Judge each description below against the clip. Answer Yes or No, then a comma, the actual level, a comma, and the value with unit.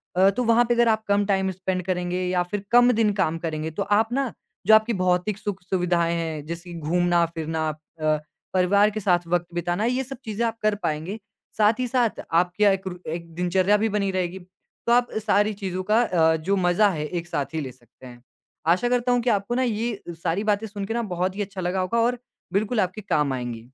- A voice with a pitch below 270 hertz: Yes, high, 190 Hz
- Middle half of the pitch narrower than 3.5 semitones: No, average, 3.8 semitones